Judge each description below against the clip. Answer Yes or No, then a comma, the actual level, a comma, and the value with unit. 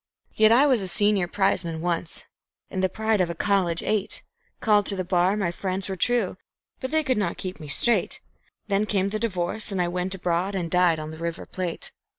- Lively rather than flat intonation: No, average, 3.2 semitones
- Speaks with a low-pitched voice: No, high, 190 Hz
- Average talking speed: No, fast, 210 wpm